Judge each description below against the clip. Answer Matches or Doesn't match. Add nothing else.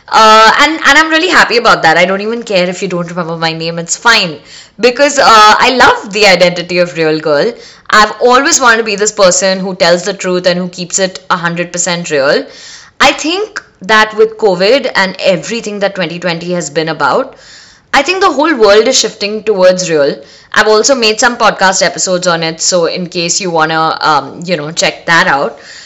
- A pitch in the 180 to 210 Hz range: Matches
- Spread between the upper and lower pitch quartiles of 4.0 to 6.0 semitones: Matches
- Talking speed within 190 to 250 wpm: Matches